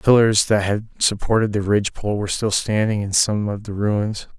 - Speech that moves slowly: No, fast, 205 wpm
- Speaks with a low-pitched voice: Yes, low, 105 Hz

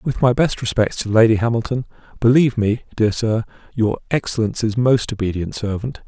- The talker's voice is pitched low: Yes, low, 115 Hz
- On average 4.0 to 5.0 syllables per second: No, 5.5 syllables/s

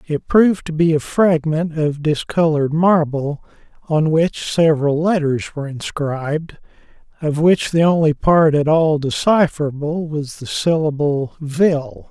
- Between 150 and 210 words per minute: No, average, 140 wpm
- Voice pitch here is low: No, medium, 155 Hz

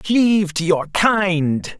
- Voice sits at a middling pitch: Yes, medium, 180 Hz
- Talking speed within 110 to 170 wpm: Yes, slow, 135 wpm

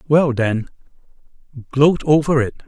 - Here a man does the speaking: Yes, male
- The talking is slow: Yes, slow, 110 wpm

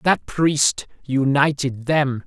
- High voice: No, low, 135 Hz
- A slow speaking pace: Yes, slow, 105 wpm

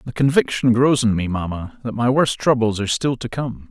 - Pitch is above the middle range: No, low, 120 Hz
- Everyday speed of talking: No, fast, 225 wpm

